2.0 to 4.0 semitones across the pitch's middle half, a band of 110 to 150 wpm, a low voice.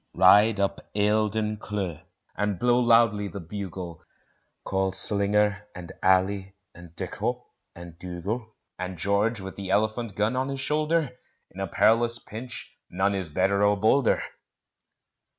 Yes: average, 2.8 semitones; slow, 135 wpm; low, 100 Hz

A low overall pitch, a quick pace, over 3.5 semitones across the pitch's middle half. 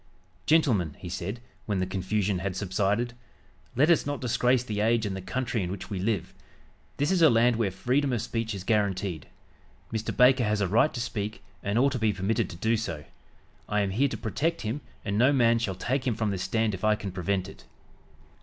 Yes: low, 110 Hz; fast, 215 wpm; average, 4.0 semitones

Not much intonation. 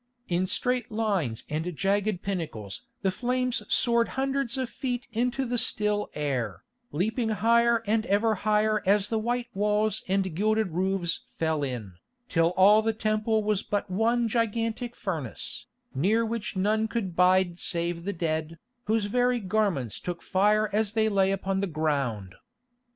No: average, 4.2 semitones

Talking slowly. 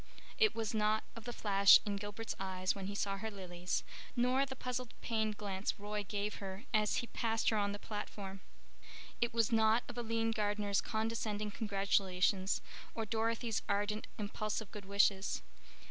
No: average, 160 wpm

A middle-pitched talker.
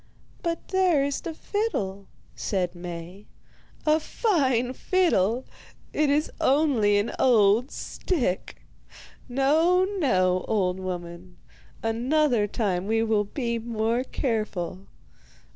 No: high, 230 Hz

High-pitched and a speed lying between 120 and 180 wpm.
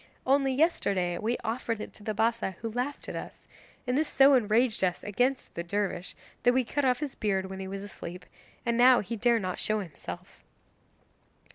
No: high, 225 Hz; average, 190 wpm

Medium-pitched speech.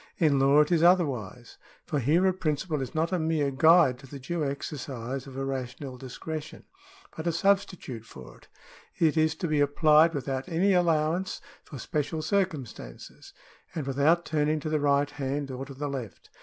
Yes: medium, 150 Hz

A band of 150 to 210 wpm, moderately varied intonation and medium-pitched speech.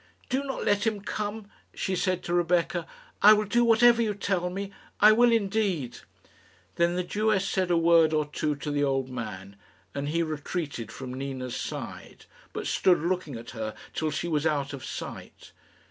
No: average, 180 wpm; wide, 6.2 semitones; medium, 170 Hz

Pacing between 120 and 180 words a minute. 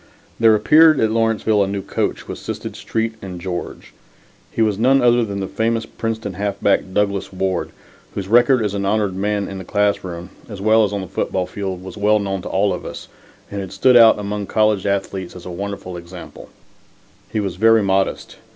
No: average, 195 wpm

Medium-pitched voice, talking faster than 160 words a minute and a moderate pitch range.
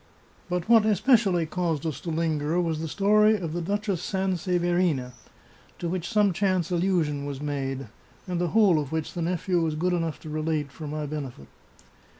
Yes: medium, 170 Hz; average, 180 wpm; average, 3.3 semitones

